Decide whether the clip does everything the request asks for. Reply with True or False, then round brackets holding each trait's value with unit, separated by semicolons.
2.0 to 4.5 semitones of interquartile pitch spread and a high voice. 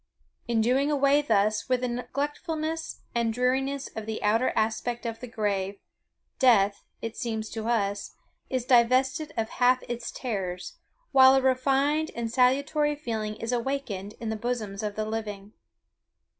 True (3.4 semitones; 240 Hz)